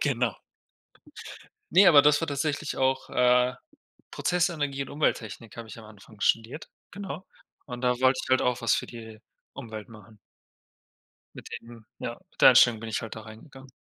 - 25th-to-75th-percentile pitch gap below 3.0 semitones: No, average, 4.0 semitones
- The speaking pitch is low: Yes, low, 125 Hz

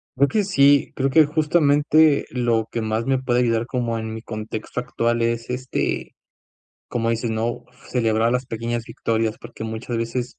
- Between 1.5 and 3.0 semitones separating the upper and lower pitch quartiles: Yes, narrow, 2.5 semitones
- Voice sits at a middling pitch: No, low, 120 Hz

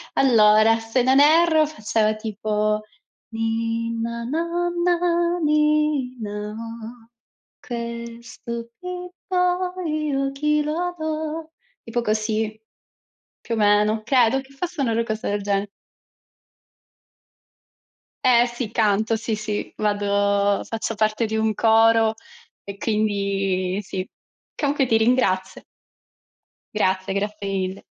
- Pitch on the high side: Yes, high, 230 Hz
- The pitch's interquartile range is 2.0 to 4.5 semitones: No, average, 5.2 semitones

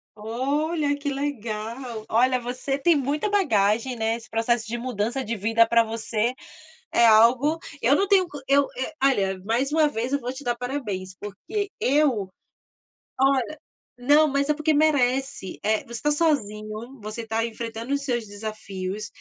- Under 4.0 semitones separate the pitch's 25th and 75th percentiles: No, average, 4.4 semitones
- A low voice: No, high, 245 Hz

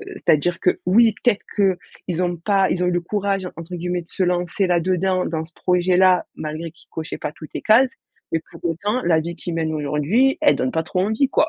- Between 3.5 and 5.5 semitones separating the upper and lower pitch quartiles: No, average, 2.8 semitones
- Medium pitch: Yes, medium, 180 Hz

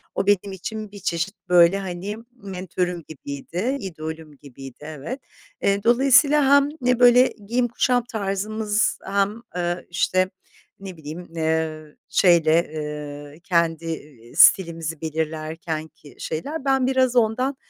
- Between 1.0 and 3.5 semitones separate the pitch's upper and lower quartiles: No, wide, 5.6 semitones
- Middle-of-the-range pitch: Yes, medium, 180 Hz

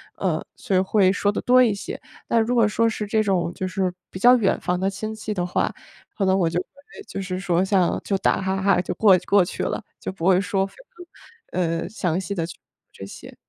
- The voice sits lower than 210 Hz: Yes, high, 190 Hz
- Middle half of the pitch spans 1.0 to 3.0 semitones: Yes, average, 2.7 semitones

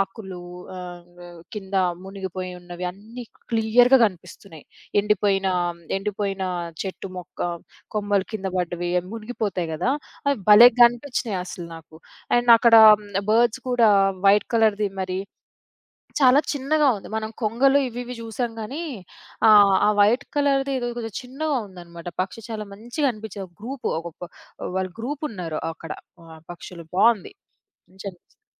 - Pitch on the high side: Yes, high, 210 Hz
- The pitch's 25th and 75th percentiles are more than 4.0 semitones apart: Yes, average, 4.6 semitones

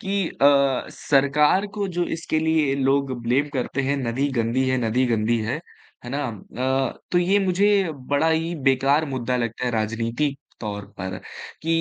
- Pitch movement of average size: Yes, average, 4.8 semitones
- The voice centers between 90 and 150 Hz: Yes, low, 135 Hz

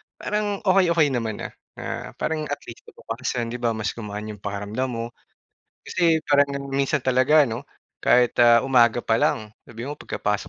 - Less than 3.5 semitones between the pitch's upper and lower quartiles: No, average, 4.5 semitones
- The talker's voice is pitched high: No, low, 125 Hz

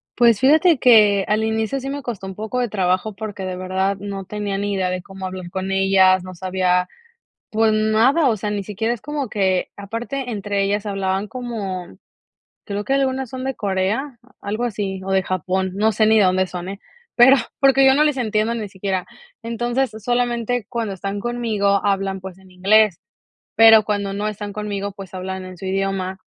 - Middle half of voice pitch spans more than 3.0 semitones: Yes, average, 3.4 semitones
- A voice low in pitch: No, high, 205 Hz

